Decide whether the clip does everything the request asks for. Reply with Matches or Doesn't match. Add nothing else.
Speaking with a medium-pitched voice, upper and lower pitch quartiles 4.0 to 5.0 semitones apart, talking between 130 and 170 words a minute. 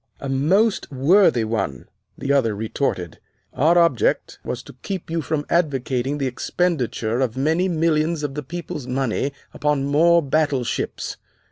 Matches